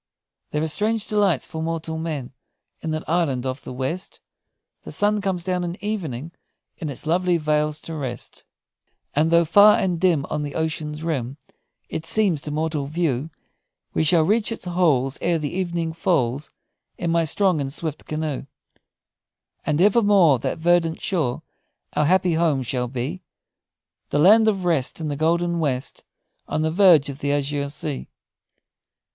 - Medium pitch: Yes, medium, 160 Hz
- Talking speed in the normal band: Yes, average, 165 wpm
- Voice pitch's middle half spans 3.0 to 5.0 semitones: Yes, average, 3.4 semitones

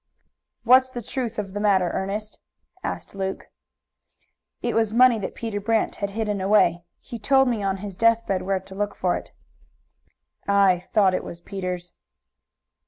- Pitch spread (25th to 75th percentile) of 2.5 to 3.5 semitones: Yes, average, 2.9 semitones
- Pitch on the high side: Yes, high, 205 Hz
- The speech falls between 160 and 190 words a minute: Yes, average, 165 wpm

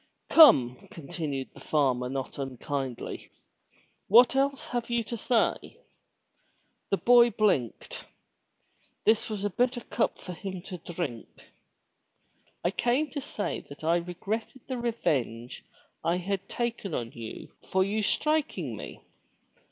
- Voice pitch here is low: No, high, 190 Hz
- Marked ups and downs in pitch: Yes, wide, 8.9 semitones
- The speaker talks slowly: Yes, slow, 130 wpm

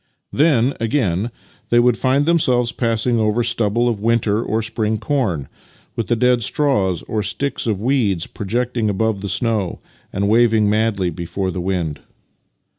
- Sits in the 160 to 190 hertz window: No, low, 110 Hz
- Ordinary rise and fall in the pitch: Yes, average, 3.2 semitones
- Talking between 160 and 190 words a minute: No, average, 150 wpm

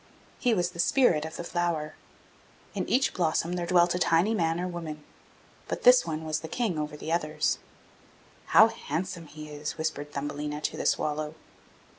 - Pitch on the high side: No, medium, 165 Hz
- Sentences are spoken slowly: No, average, 175 wpm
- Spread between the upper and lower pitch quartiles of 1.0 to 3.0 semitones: Yes, narrow, 2.6 semitones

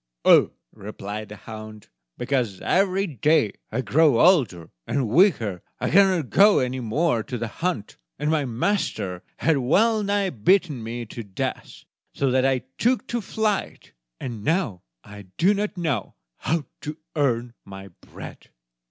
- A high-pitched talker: No, low, 130 Hz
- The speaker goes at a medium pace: Yes, average, 150 wpm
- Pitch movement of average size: No, wide, 8.8 semitones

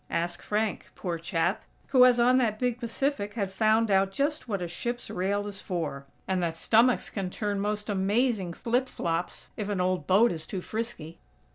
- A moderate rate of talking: Yes, average, 185 wpm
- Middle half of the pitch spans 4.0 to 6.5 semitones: Yes, average, 4.3 semitones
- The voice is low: No, high, 205 Hz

